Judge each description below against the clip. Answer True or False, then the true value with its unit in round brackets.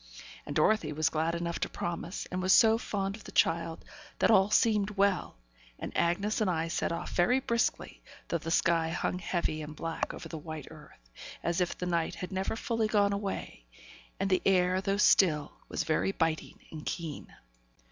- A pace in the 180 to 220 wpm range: True (190 wpm)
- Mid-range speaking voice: True (180 Hz)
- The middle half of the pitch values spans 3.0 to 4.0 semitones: True (3.5 semitones)